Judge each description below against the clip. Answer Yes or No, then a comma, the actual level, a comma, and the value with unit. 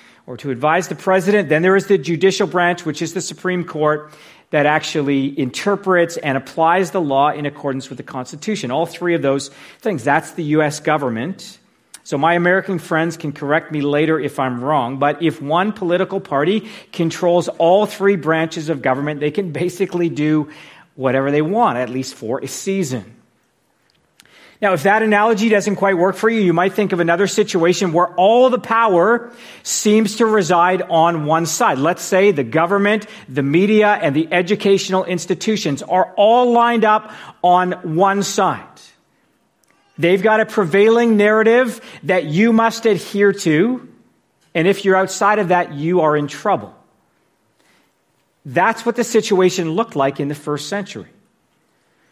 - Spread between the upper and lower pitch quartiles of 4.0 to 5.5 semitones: Yes, average, 5.0 semitones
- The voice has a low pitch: No, medium, 175 Hz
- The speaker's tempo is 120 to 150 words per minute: No, average, 165 wpm